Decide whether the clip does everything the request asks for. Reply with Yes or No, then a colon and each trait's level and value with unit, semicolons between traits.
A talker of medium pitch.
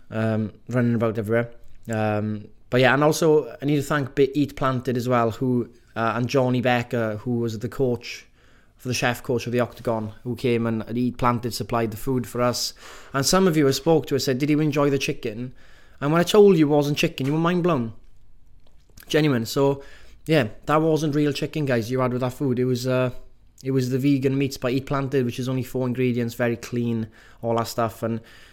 No: low, 125 Hz